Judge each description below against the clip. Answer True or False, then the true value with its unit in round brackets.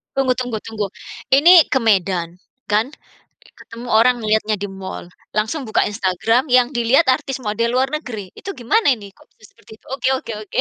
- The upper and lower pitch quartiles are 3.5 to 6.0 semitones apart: True (3.8 semitones)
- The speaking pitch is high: True (230 Hz)